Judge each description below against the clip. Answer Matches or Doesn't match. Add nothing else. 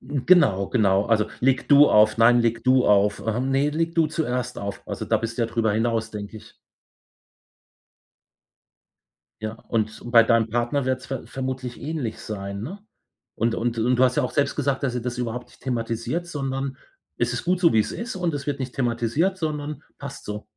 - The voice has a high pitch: Doesn't match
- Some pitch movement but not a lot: Matches